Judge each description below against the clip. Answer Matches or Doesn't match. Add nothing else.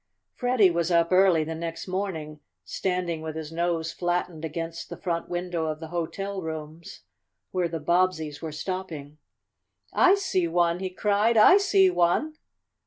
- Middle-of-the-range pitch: Matches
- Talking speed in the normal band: Matches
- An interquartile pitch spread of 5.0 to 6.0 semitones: Doesn't match